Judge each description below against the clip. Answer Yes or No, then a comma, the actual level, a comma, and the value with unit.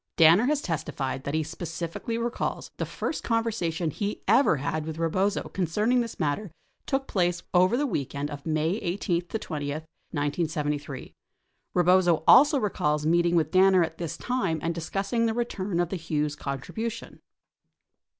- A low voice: No, medium, 175 Hz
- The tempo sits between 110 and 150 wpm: No, average, 160 wpm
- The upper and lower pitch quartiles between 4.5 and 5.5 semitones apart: Yes, average, 5.1 semitones